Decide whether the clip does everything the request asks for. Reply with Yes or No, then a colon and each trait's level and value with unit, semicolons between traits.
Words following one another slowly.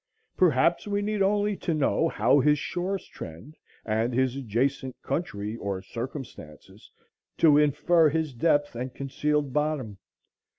Yes: slow, 130 wpm